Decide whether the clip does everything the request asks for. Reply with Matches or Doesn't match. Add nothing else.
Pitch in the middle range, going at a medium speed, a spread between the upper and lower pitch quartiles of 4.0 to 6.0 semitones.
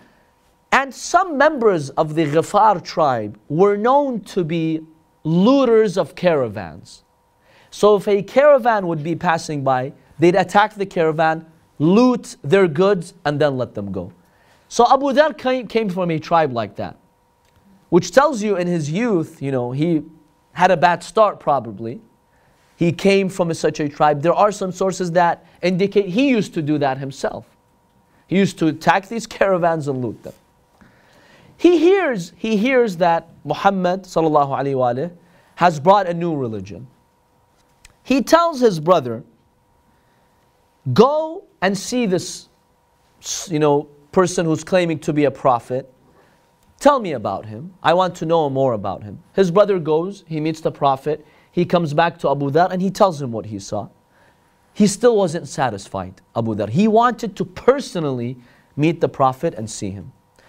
Matches